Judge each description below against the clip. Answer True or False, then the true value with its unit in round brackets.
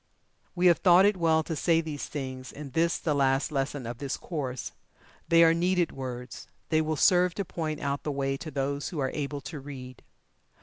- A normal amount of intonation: True (3.5 semitones)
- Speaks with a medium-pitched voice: True (150 Hz)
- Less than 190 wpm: False (205 wpm)